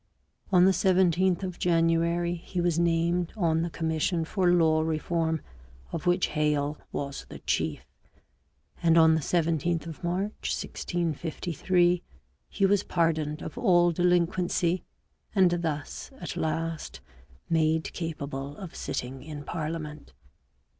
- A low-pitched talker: No, medium, 165 Hz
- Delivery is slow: Yes, slow, 125 wpm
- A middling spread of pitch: No, narrow, 1.9 semitones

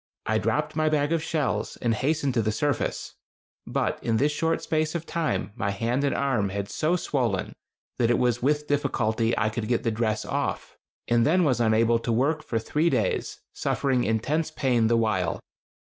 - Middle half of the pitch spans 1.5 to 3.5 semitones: No, average, 5.0 semitones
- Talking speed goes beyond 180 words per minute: Yes, average, 190 wpm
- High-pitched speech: No, low, 125 Hz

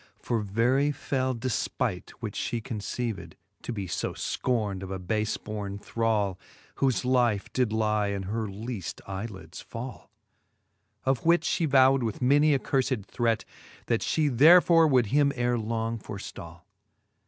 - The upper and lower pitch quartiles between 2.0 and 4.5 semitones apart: Yes, average, 4.2 semitones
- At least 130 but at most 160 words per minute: Yes, average, 150 wpm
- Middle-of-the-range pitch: No, low, 115 Hz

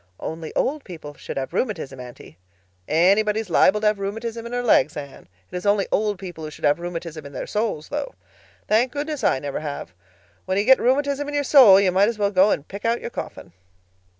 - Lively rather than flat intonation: Yes, wide, 6.5 semitones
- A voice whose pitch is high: Yes, high, 200 Hz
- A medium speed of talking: No, fast, 210 wpm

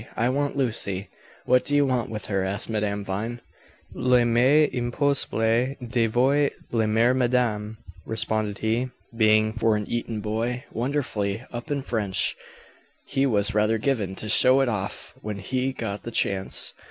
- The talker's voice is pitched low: Yes, low, 115 Hz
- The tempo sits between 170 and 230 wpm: No, average, 155 wpm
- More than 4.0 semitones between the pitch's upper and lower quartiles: No, average, 3.1 semitones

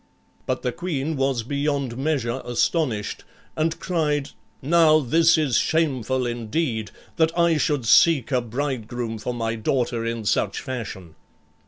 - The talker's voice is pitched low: Yes, low, 130 Hz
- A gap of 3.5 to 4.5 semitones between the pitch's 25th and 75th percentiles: No, average, 4.9 semitones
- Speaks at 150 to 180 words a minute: No, slow, 135 wpm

